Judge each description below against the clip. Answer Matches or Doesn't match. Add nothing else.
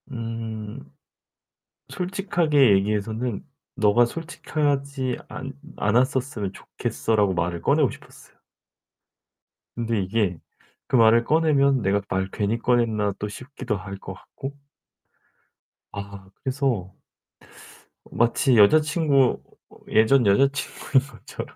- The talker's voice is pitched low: Matches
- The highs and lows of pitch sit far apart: Doesn't match